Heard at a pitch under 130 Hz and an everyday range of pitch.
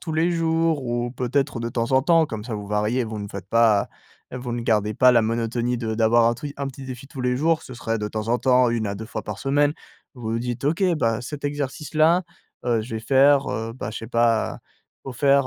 Yes: low, 120 Hz; average, 3.5 semitones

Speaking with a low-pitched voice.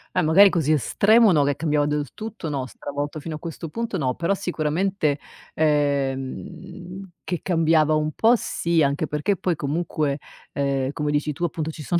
No: medium, 155 Hz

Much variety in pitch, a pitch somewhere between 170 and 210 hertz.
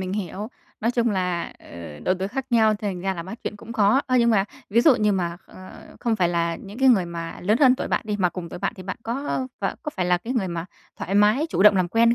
No: average, 4.3 semitones; high, 200 Hz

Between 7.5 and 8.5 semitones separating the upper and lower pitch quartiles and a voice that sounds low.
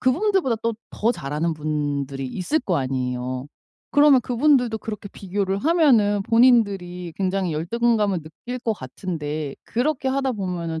No: wide, 7.9 semitones; high, 195 Hz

